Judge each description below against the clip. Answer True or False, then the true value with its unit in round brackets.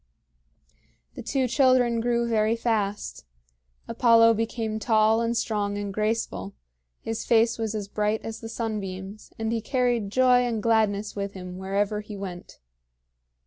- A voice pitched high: True (220 Hz)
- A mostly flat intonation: True (2.2 semitones)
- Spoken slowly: False (145 wpm)